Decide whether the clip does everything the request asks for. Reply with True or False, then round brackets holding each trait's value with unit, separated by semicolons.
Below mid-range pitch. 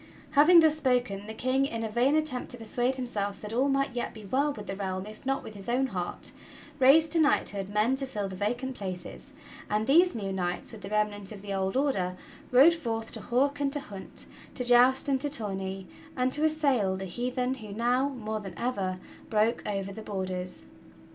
False (230 Hz)